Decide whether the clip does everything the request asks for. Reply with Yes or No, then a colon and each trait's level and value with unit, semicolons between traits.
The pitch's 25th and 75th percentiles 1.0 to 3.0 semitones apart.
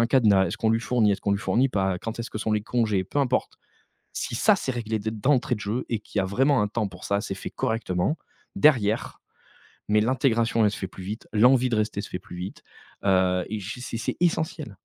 No: average, 3.5 semitones